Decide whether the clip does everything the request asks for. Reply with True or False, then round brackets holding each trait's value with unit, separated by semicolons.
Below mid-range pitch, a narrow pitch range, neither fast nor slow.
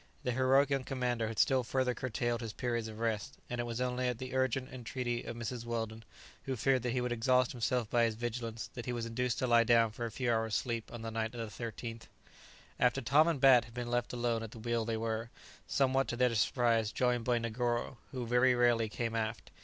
False (120 Hz; 1.7 semitones; 230 wpm)